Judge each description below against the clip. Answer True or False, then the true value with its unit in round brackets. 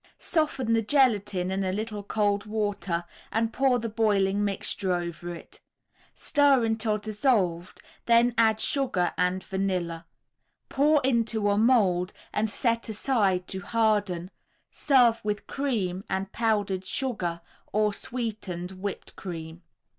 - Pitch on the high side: True (210 Hz)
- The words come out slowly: True (125 wpm)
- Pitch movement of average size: True (3.6 semitones)